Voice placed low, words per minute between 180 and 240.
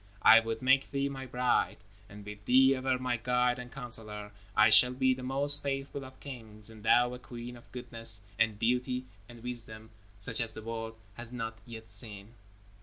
Yes: low, 120 Hz; average, 185 wpm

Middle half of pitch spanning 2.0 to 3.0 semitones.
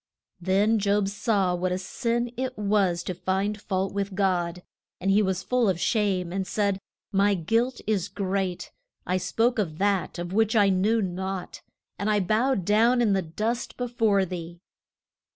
Yes: average, 2.7 semitones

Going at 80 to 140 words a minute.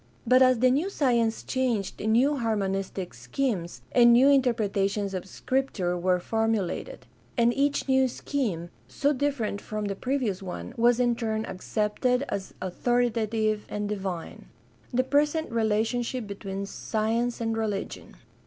Yes: slow, 135 wpm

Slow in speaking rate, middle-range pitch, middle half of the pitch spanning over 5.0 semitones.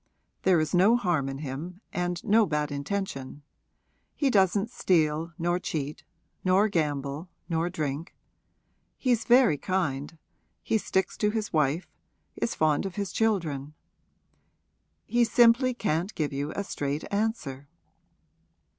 Yes: slow, 130 wpm; medium, 175 Hz; wide, 5.4 semitones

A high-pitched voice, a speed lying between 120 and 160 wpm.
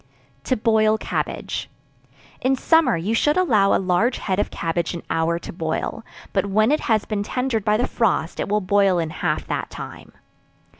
No: high, 210 Hz; average, 185 wpm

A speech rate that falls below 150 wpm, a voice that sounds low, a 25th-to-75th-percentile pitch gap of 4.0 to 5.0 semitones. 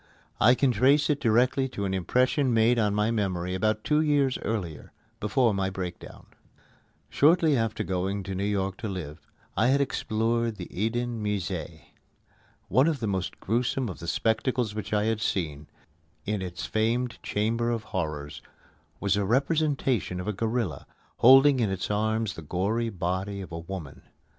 No: average, 165 wpm; low, 110 Hz; average, 4.3 semitones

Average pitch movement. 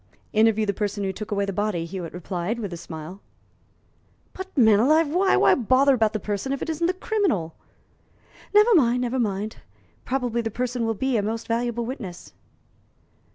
Yes: average, 4.6 semitones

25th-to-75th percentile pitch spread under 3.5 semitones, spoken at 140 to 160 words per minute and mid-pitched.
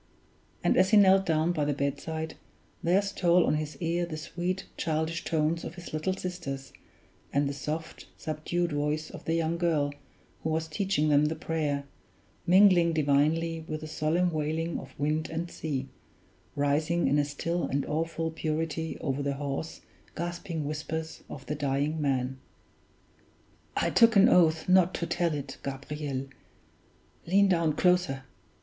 Yes: narrow, 2.6 semitones; average, 155 wpm; medium, 160 Hz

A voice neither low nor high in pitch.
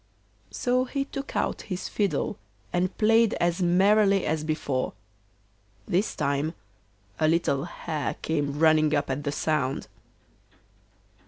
Yes: medium, 165 Hz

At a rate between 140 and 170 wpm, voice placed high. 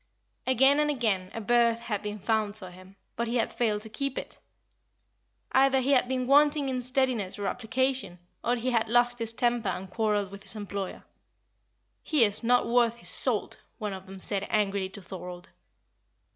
No: average, 185 wpm; high, 225 Hz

